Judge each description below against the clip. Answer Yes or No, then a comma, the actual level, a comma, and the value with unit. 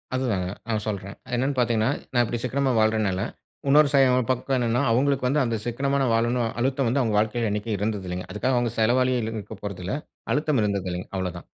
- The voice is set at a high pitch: No, low, 115 Hz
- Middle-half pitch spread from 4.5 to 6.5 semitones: No, average, 3.5 semitones